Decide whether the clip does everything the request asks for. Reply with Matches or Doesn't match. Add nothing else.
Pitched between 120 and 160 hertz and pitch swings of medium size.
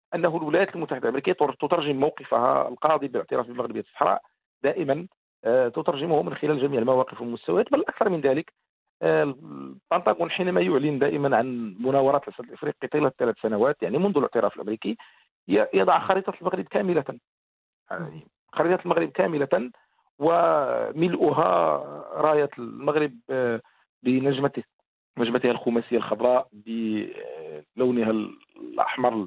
Doesn't match